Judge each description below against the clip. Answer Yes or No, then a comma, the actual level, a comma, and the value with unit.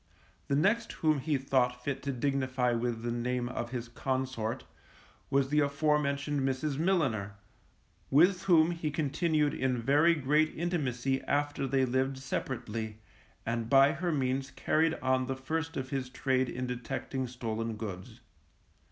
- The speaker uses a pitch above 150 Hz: No, low, 135 Hz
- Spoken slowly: No, average, 150 wpm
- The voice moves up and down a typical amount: Yes, average, 3.2 semitones